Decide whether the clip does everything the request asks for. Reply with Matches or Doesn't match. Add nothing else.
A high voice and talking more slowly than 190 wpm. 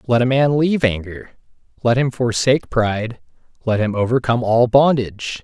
Doesn't match